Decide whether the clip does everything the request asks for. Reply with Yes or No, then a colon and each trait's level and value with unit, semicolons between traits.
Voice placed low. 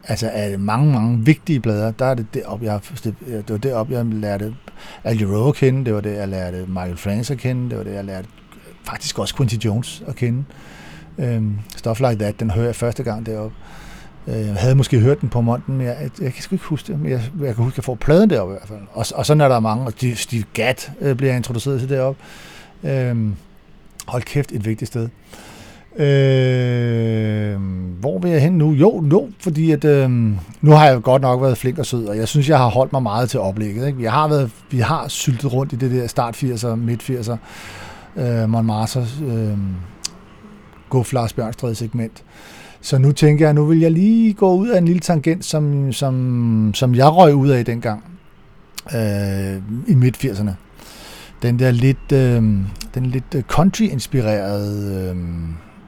Yes: low, 120 Hz